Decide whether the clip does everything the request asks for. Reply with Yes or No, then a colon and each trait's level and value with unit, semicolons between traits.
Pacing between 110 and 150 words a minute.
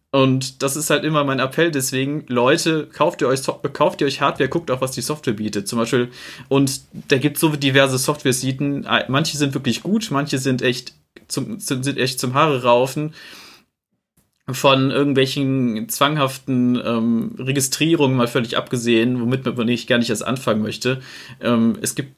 No: average, 165 wpm